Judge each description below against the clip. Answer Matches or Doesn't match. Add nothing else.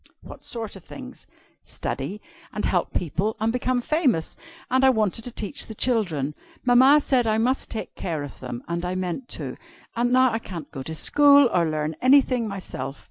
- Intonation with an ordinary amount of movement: Doesn't match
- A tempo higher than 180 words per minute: Matches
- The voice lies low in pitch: Doesn't match